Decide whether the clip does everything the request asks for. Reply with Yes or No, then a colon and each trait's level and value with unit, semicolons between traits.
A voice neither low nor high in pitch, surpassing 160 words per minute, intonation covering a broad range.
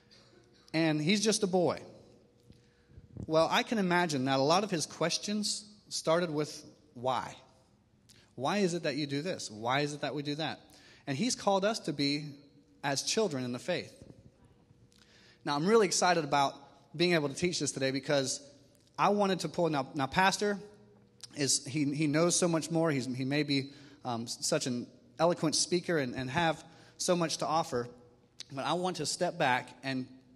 No: medium, 150 Hz; average, 180 wpm; average, 4.4 semitones